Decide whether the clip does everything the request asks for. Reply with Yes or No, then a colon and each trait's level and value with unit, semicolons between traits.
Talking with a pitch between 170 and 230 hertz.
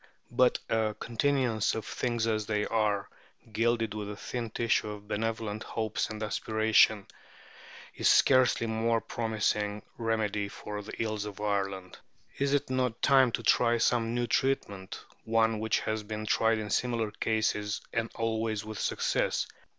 No: low, 110 Hz